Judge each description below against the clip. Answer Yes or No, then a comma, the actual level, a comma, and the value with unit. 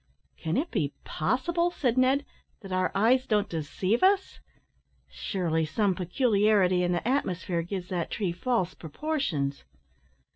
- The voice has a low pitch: No, high, 195 Hz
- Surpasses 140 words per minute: No, slow, 135 wpm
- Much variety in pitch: Yes, wide, 6.7 semitones